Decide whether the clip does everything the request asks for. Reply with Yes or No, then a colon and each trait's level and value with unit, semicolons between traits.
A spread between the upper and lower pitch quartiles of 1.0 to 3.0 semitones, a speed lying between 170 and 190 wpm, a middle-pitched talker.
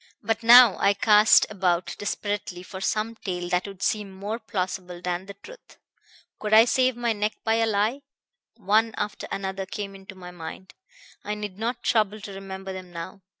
No: narrow, 2.6 semitones; average, 180 wpm; high, 200 Hz